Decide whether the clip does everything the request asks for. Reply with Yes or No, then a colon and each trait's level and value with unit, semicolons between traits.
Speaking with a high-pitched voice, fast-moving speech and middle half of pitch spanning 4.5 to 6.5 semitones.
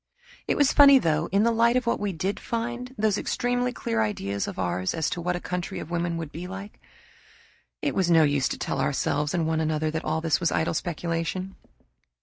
No: medium, 170 Hz; fast, 215 wpm; average, 5.0 semitones